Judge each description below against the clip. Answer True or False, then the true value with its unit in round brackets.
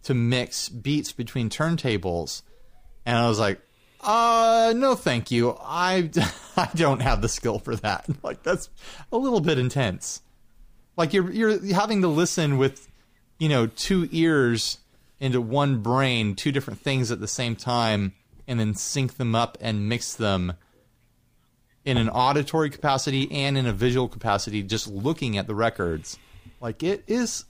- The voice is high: False (125 Hz)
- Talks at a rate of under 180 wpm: True (160 wpm)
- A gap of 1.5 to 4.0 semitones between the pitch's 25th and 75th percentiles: False (4.5 semitones)